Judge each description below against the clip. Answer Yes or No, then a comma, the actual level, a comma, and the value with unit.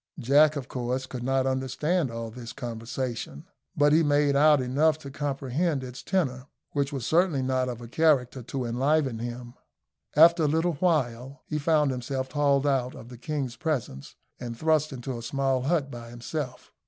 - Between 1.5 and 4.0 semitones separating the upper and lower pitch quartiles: Yes, average, 3.4 semitones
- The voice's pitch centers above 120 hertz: Yes, low, 135 Hz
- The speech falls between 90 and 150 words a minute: No, average, 175 wpm